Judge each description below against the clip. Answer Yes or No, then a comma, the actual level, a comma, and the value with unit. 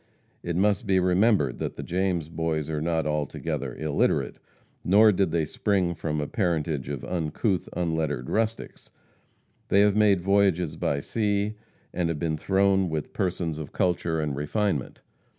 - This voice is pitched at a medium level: No, very low, 85 Hz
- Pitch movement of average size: Yes, average, 4.1 semitones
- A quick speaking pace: No, average, 150 wpm